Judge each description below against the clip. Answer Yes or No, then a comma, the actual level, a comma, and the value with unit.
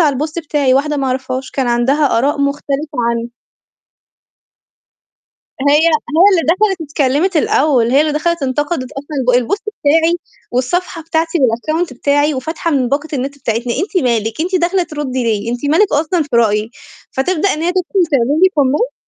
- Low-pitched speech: No, very high, 290 Hz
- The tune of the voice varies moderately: Yes, average, 4.2 semitones